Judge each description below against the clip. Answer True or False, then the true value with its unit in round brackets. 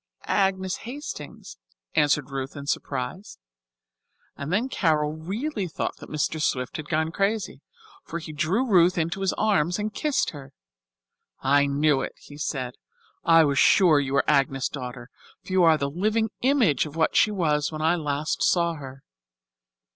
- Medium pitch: True (160 Hz)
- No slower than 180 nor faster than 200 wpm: False (160 wpm)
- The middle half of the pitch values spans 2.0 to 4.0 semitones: False (4.9 semitones)